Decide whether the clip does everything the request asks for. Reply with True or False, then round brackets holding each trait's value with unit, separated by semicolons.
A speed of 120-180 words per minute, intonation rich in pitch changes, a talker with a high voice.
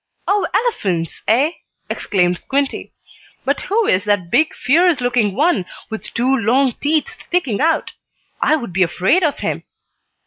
True (145 wpm; 7.7 semitones; 255 Hz)